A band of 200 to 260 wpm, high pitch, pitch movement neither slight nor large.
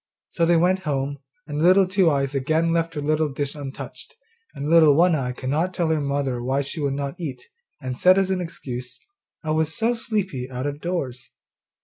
No: fast, 205 wpm; medium, 150 Hz; average, 3.7 semitones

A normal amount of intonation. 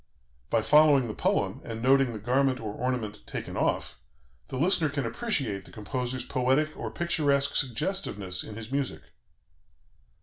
Yes: average, 4.0 semitones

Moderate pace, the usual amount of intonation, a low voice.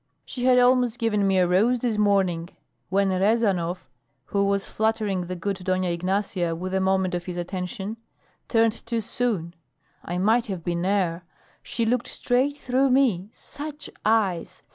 No: average, 160 wpm; average, 4.1 semitones; high, 200 Hz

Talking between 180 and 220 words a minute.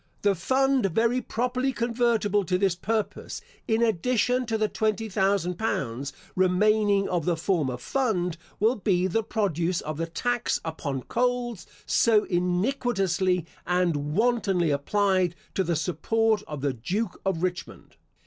No: average, 140 wpm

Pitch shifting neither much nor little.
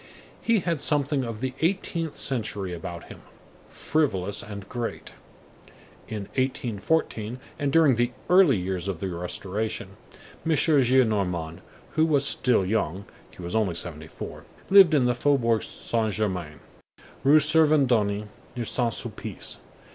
No: wide, 6.8 semitones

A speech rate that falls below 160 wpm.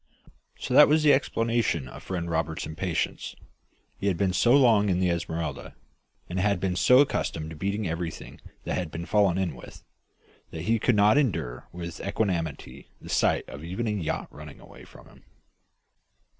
No: average, 175 wpm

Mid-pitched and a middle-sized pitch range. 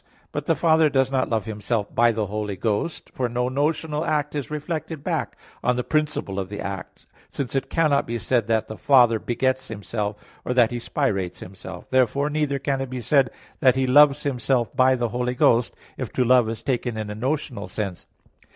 No: low, 125 Hz; average, 4.0 semitones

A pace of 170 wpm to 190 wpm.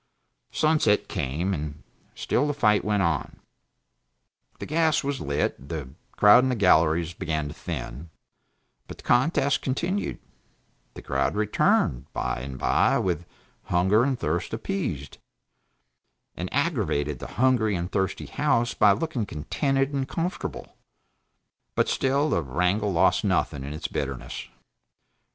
No: slow, 135 wpm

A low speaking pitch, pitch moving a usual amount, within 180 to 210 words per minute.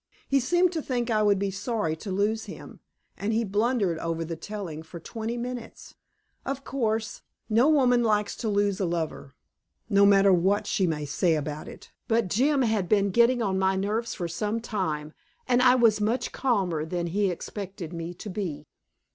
No: high, 205 Hz; average, 4.8 semitones; average, 185 wpm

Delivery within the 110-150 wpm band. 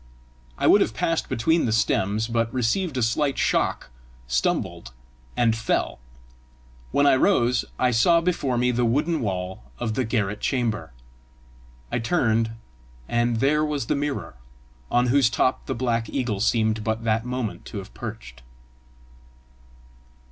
Yes: average, 145 wpm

